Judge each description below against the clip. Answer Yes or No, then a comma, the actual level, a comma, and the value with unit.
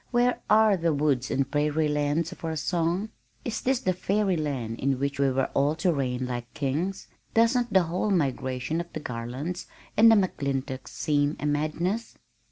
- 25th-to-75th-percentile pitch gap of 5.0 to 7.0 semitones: Yes, average, 5.3 semitones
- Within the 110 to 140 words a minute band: No, average, 175 wpm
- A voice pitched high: No, medium, 155 Hz